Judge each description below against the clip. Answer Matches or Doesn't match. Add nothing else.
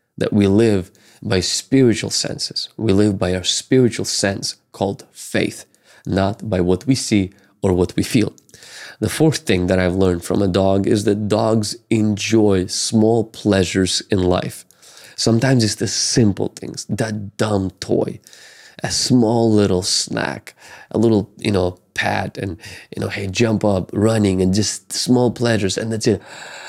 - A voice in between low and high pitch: Doesn't match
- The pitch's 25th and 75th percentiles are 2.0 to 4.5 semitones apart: Matches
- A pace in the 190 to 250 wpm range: Doesn't match